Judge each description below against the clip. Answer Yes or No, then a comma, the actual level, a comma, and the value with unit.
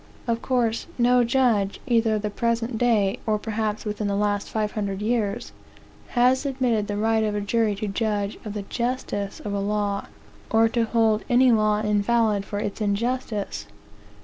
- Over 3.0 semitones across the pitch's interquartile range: No, narrow, 2.4 semitones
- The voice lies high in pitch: Yes, high, 215 Hz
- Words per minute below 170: No, average, 175 wpm